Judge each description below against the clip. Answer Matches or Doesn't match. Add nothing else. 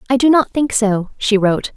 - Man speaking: Doesn't match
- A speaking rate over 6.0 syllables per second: Doesn't match